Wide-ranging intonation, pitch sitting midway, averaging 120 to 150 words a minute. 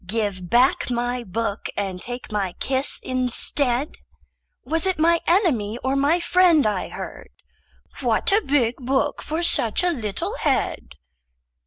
No: wide, 6.1 semitones; very high, 250 Hz; average, 140 wpm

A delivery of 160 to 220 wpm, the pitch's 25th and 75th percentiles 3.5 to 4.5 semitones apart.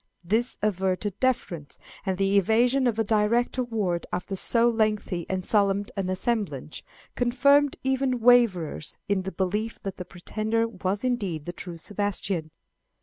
No: average, 145 wpm; average, 4.1 semitones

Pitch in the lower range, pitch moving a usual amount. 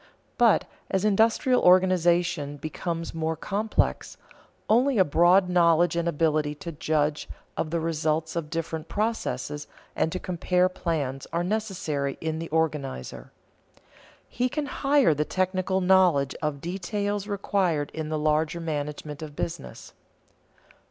No: medium, 170 Hz; average, 3.6 semitones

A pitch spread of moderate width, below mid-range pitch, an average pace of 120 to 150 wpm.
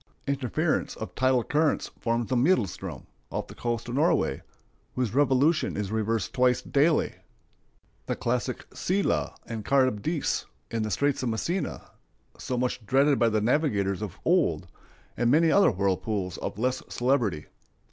Yes: average, 4.6 semitones; low, 125 Hz; average, 145 wpm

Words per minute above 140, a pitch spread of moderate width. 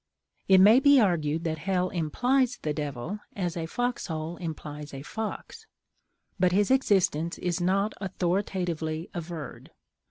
No: slow, 135 wpm; average, 4.2 semitones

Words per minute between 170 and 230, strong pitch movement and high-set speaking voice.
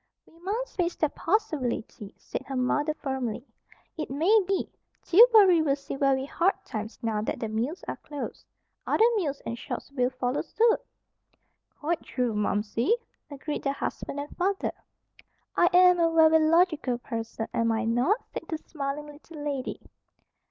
No: average, 155 wpm; wide, 5.7 semitones; very high, 290 Hz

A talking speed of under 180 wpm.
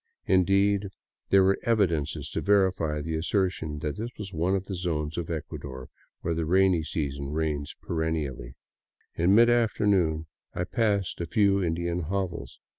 Yes: average, 145 wpm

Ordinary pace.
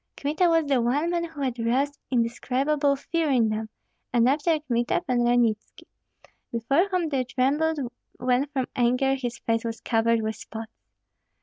Yes: average, 160 wpm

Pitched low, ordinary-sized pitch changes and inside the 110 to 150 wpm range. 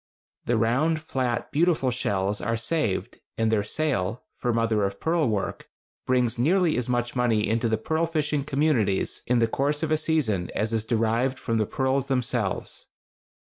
No: low, 120 Hz; average, 4.9 semitones; average, 170 wpm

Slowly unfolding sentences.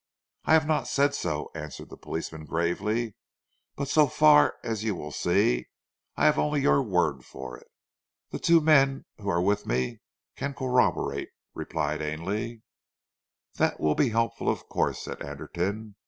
No: average, 155 wpm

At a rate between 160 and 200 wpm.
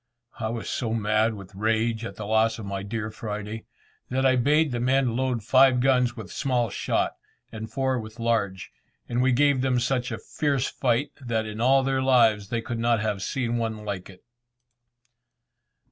Yes: average, 185 wpm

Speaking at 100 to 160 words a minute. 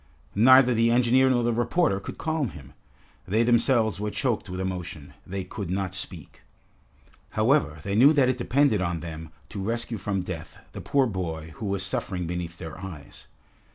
No: average, 175 wpm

